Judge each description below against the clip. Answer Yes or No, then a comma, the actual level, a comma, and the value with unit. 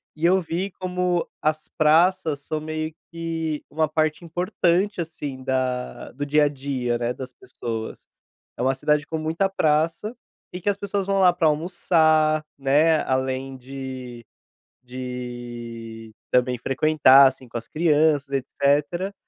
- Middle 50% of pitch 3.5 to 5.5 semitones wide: Yes, average, 4.3 semitones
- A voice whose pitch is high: No, medium, 150 Hz